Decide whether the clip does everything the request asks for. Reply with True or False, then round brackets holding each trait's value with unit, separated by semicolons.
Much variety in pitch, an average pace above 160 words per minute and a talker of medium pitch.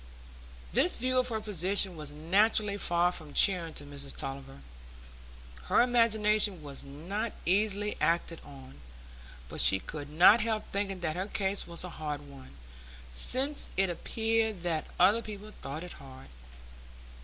False (5.9 semitones; 145 wpm; 180 Hz)